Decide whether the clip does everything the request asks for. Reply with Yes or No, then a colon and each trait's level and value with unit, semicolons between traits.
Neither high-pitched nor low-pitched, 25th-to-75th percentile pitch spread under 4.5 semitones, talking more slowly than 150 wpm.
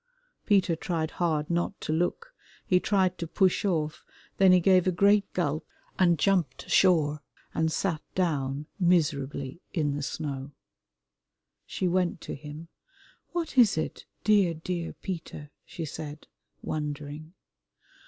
Yes: medium, 165 Hz; average, 3.5 semitones; slow, 135 wpm